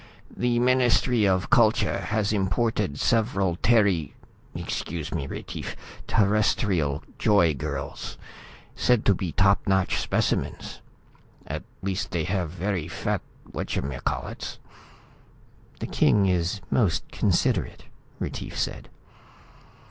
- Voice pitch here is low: Yes, very low, 95 Hz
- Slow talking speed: Yes, slow, 100 wpm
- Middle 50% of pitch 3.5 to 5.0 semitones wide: Yes, average, 3.9 semitones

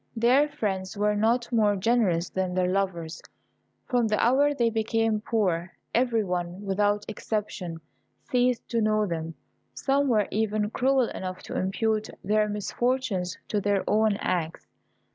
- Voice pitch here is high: Yes, high, 210 Hz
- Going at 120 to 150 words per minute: Yes, average, 145 wpm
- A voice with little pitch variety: No, average, 3.6 semitones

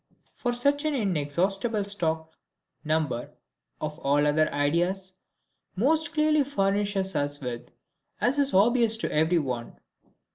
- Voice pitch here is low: No, high, 190 Hz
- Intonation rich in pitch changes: Yes, wide, 7.9 semitones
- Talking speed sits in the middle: No, slow, 130 wpm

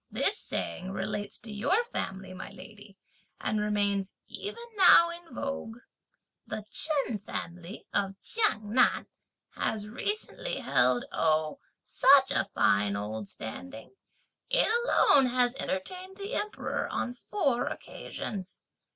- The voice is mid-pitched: No, high, 215 Hz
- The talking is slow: Yes, slow, 120 wpm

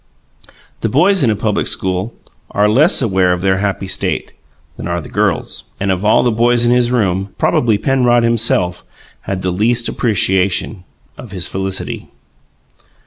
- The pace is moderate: Yes, average, 160 wpm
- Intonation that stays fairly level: No, average, 4.1 semitones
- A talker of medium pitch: No, low, 105 Hz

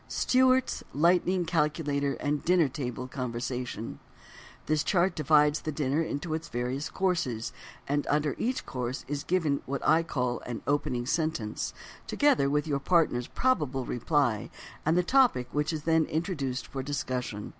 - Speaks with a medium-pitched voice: Yes, medium, 145 Hz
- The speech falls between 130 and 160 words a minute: Yes, average, 145 wpm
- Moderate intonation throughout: Yes, average, 4.3 semitones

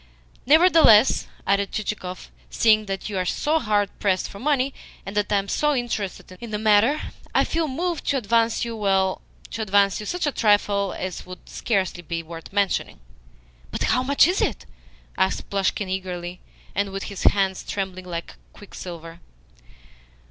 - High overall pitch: Yes, high, 205 Hz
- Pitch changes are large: No, average, 3.7 semitones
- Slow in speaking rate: No, average, 165 wpm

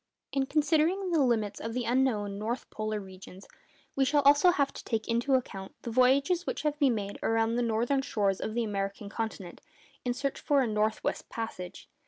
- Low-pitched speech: No, high, 235 Hz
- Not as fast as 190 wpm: No, average, 200 wpm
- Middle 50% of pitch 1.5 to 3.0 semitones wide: No, average, 4.6 semitones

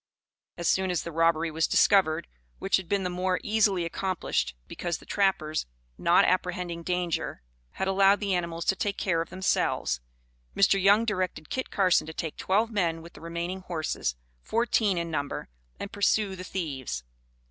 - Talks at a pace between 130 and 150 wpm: No, average, 170 wpm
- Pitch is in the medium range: Yes, medium, 180 Hz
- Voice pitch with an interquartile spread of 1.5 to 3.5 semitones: Yes, average, 2.8 semitones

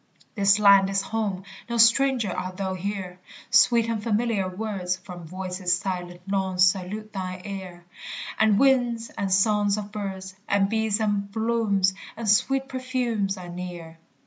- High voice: Yes, high, 200 Hz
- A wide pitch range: No, average, 3.0 semitones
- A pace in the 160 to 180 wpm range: No, average, 145 wpm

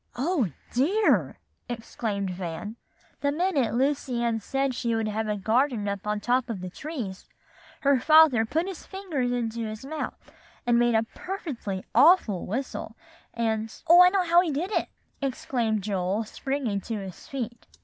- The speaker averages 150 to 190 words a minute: Yes, average, 165 wpm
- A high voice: Yes, high, 240 Hz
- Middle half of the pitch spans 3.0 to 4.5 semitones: No, average, 5.1 semitones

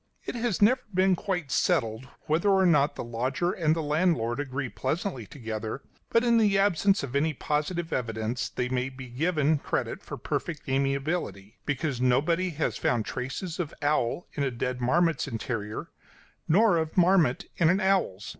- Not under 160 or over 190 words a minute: Yes, average, 165 wpm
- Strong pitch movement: Yes, wide, 6.1 semitones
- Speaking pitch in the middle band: Yes, medium, 150 Hz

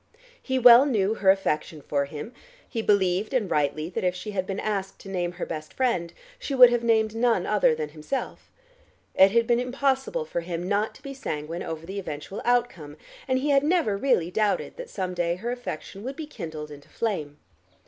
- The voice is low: No, high, 200 Hz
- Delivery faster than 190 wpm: Yes, average, 200 wpm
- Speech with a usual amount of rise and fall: No, wide, 6.4 semitones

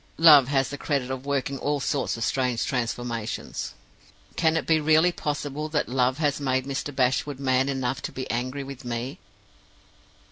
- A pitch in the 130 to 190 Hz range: Yes, low, 135 Hz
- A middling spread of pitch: No, narrow, 2.3 semitones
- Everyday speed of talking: Yes, average, 170 wpm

